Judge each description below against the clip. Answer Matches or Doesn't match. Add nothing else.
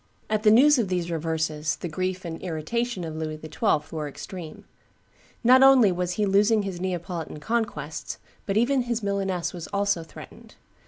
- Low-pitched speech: Doesn't match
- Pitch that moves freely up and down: Doesn't match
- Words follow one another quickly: Doesn't match